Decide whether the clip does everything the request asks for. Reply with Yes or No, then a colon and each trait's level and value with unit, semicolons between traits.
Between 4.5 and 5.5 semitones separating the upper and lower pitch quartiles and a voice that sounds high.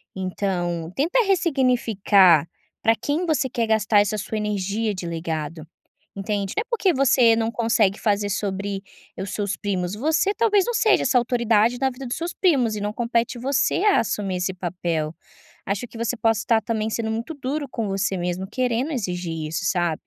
Yes: average, 4.9 semitones; high, 220 Hz